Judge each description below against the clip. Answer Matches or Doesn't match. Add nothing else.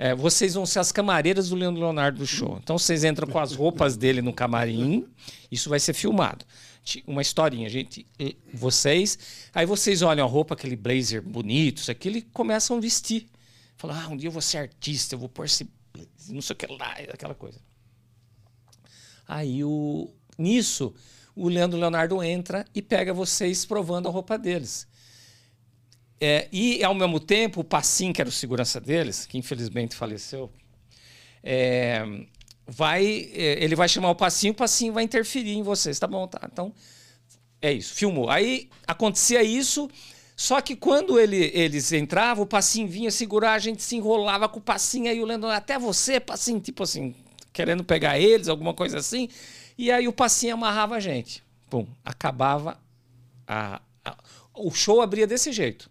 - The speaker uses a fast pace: Doesn't match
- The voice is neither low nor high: Matches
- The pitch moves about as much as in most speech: Doesn't match